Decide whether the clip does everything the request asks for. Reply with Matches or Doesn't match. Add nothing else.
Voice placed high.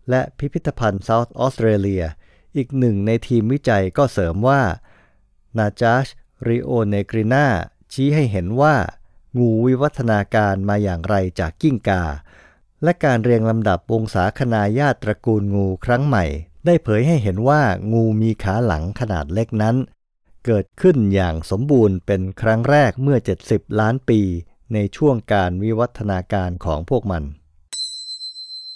Doesn't match